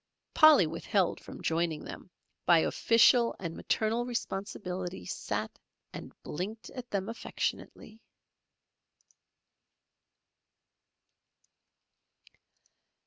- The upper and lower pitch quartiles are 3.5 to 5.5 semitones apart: Yes, average, 5.2 semitones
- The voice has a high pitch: Yes, high, 200 Hz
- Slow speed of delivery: Yes, slow, 75 wpm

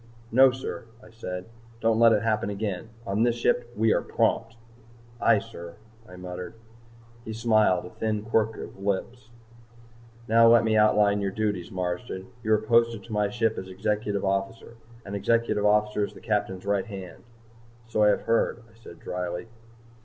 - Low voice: Yes, low, 105 Hz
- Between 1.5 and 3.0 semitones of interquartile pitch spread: Yes, narrow, 2.6 semitones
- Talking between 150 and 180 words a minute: Yes, average, 175 wpm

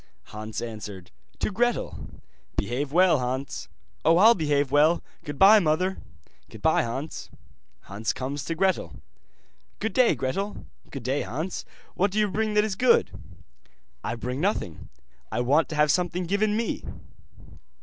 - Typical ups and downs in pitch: No, wide, 7.2 semitones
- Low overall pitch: No, medium, 155 Hz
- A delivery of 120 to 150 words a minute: Yes, average, 140 wpm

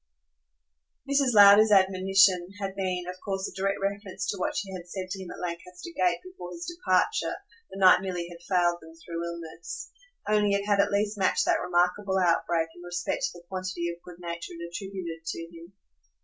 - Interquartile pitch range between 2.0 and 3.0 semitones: Yes, narrow, 2.4 semitones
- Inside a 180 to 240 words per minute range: Yes, average, 190 wpm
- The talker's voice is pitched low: No, medium, 185 Hz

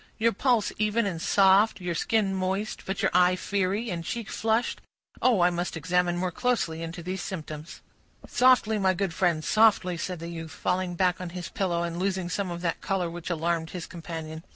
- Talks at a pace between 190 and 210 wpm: Yes, average, 195 wpm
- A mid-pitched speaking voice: Yes, medium, 180 Hz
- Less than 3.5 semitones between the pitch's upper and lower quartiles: Yes, average, 2.8 semitones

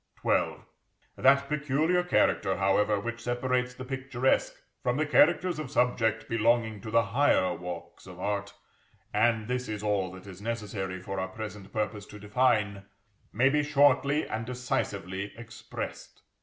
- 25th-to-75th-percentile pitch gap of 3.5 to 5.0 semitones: Yes, average, 4.2 semitones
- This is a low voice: Yes, low, 115 Hz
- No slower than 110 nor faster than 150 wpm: Yes, average, 145 wpm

